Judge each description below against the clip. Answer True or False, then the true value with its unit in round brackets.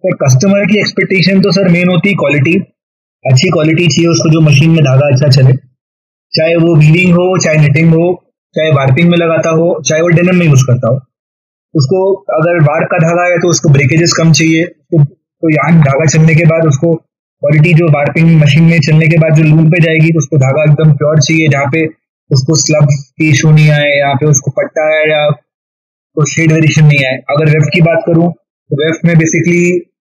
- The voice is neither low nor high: True (160 Hz)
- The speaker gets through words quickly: True (210 wpm)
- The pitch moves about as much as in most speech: False (2.3 semitones)